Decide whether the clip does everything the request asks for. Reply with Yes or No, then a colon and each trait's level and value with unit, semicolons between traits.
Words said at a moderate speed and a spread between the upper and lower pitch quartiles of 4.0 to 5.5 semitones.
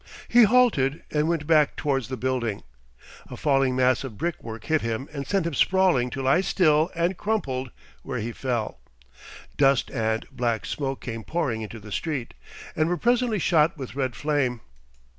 Yes: average, 175 wpm; average, 5.2 semitones